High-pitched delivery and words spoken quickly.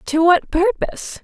No: very high, 360 Hz; average, 145 wpm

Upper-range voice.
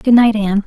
Yes: high, 215 Hz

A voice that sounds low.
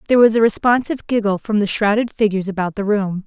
No: high, 210 Hz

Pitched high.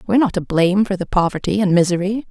Yes: high, 195 Hz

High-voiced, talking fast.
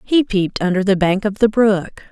Yes: high, 200 Hz; fast, 225 wpm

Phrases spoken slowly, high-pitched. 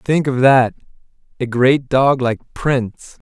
No: slow, 125 wpm; low, 130 Hz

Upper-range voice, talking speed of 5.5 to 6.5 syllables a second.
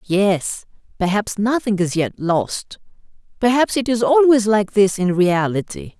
No: high, 210 Hz; 4.1 syllables/s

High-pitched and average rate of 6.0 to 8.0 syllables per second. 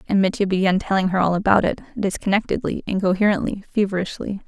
Yes: high, 195 Hz; 6.4 syllables/s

